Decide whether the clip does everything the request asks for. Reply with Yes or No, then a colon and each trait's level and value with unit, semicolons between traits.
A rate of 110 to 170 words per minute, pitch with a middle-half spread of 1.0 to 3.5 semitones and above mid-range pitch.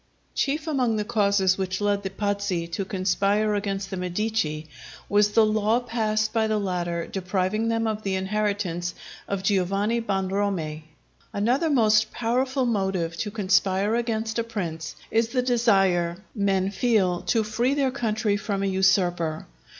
Yes: average, 150 wpm; average, 2.8 semitones; high, 205 Hz